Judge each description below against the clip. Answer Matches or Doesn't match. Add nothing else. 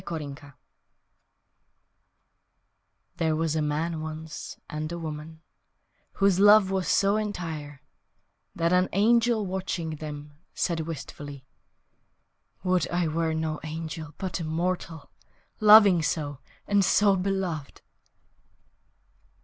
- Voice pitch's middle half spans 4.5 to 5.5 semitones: Doesn't match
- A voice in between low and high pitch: Matches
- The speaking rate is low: Matches